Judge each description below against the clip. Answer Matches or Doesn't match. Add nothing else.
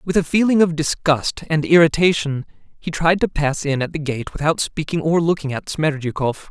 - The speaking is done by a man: Matches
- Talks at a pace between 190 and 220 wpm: Matches